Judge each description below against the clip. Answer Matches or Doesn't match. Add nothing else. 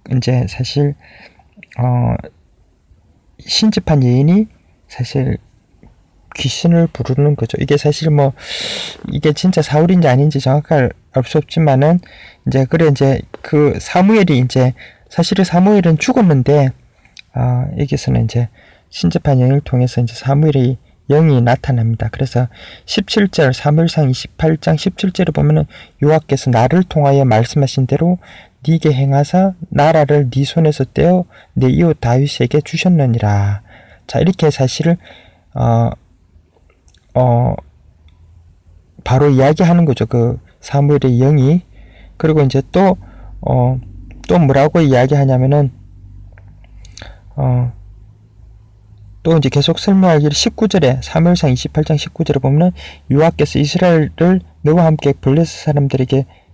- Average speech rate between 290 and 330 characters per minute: Doesn't match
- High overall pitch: Doesn't match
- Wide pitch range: Doesn't match